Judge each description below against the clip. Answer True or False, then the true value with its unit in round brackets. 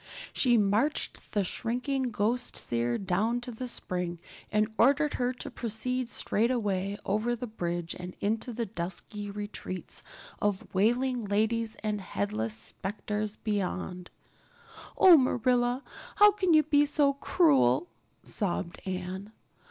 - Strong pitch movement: False (4.8 semitones)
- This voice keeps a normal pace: False (125 wpm)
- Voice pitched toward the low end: False (215 Hz)